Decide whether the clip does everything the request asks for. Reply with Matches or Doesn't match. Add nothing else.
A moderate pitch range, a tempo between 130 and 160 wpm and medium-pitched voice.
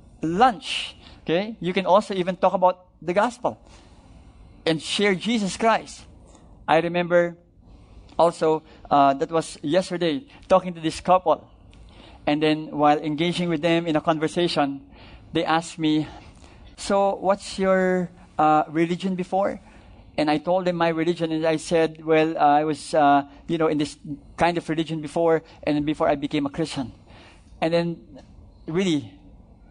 Matches